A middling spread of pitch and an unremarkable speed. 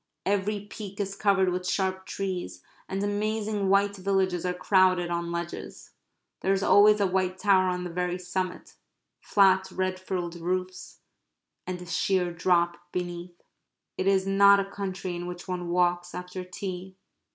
No: narrow, 1.7 semitones; average, 155 wpm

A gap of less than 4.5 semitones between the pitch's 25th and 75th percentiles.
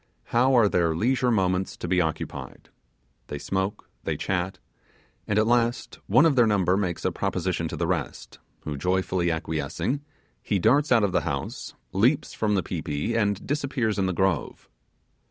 No: average, 4.9 semitones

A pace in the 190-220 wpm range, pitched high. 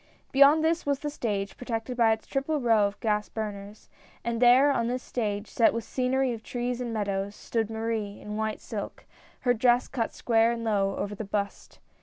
Yes: average, 200 wpm; high, 230 Hz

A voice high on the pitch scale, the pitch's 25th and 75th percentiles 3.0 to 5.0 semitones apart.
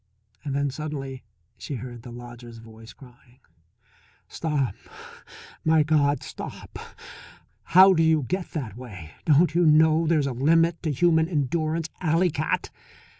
No: medium, 150 Hz; average, 4.2 semitones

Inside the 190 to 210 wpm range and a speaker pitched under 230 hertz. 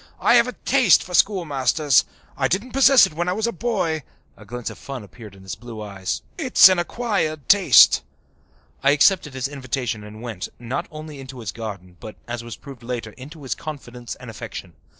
Yes: average, 195 wpm; low, 135 Hz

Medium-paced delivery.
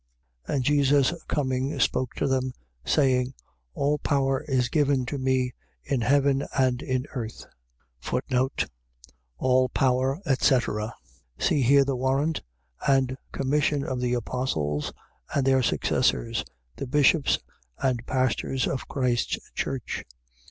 No: slow, 120 wpm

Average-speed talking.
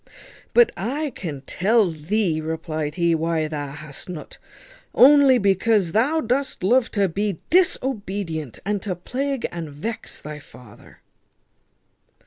No: slow, 120 wpm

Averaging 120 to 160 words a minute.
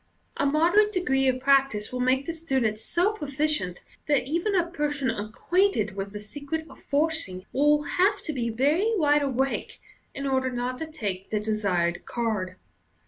No: average, 170 wpm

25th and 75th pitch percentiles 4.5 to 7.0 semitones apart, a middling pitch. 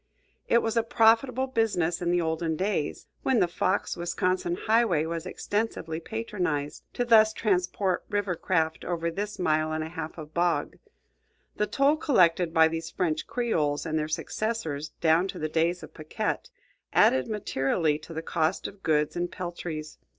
Yes: average, 4.8 semitones; medium, 175 Hz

